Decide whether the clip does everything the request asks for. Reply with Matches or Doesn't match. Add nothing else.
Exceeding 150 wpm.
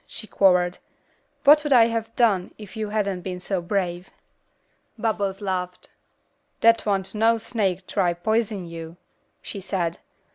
Doesn't match